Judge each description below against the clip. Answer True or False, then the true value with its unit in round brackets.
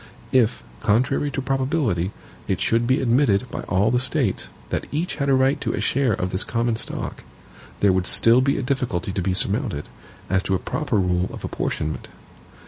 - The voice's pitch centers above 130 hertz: False (115 Hz)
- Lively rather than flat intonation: True (5.7 semitones)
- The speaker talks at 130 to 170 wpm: False (190 wpm)